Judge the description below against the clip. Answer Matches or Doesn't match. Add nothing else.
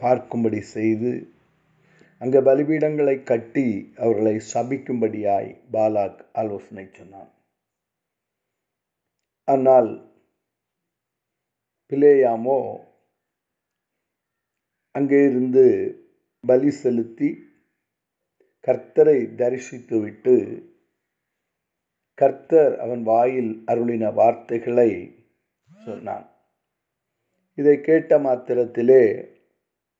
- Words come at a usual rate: Doesn't match